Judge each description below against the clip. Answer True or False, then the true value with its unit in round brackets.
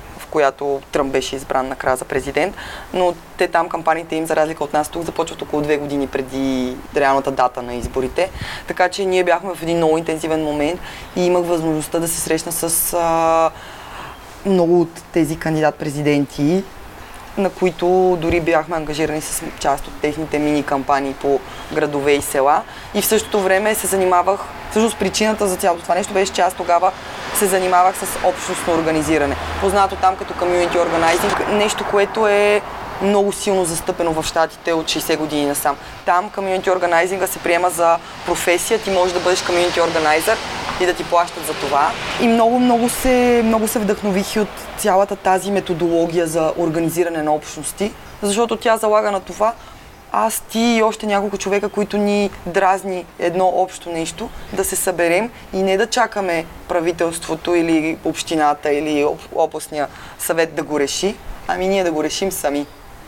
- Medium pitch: True (175 Hz)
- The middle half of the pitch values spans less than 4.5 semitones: True (3.7 semitones)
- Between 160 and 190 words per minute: True (165 wpm)